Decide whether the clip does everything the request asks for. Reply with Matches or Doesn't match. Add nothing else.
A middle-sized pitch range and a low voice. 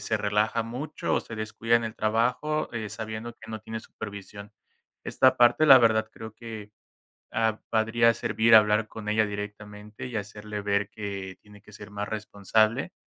Doesn't match